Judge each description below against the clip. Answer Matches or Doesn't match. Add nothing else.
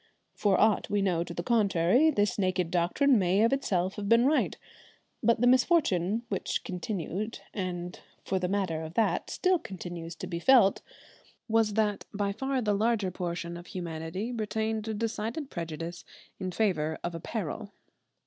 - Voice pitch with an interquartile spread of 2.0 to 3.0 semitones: Doesn't match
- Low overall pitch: Doesn't match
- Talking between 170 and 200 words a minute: Doesn't match